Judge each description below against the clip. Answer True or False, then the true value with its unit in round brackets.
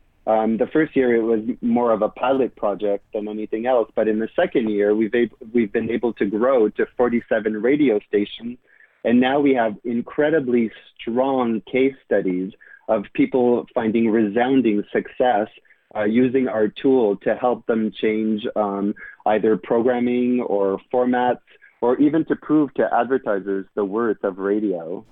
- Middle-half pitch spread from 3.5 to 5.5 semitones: False (2.8 semitones)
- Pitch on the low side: True (115 Hz)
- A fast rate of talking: False (160 wpm)